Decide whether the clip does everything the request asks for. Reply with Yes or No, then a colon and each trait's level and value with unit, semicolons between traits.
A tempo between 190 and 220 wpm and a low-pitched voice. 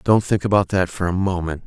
No: fast, 250 wpm; very low, 90 Hz